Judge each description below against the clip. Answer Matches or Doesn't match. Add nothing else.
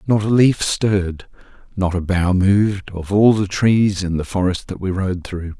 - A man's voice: Matches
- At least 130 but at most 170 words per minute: Doesn't match